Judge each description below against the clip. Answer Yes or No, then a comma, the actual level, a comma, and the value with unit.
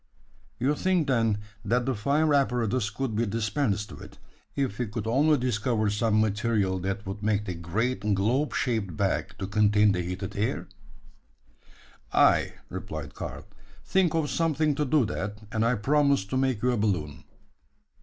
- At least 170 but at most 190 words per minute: No, average, 160 wpm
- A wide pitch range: No, average, 4.6 semitones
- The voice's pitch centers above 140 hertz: No, low, 110 Hz